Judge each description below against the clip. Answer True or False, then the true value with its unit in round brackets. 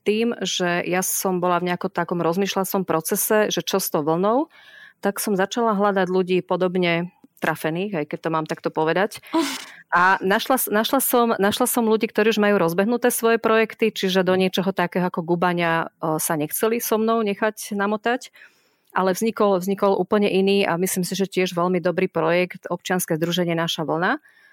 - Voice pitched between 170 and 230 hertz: True (190 Hz)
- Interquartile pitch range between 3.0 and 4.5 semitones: True (3.7 semitones)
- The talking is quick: True (170 wpm)